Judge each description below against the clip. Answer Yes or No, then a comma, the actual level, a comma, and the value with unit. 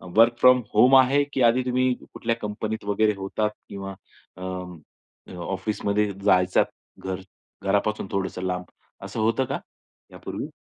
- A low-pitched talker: Yes, low, 105 Hz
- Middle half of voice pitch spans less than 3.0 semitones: No, average, 3.3 semitones